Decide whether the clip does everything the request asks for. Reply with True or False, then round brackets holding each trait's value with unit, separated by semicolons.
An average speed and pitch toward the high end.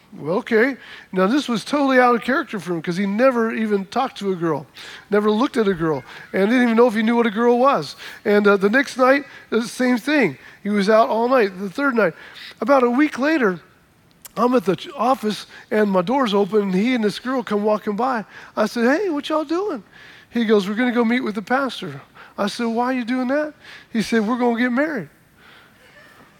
False (230 wpm; 230 Hz)